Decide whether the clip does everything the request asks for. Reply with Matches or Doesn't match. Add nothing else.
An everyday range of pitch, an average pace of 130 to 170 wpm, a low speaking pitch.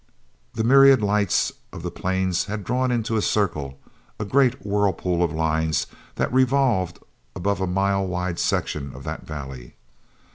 Matches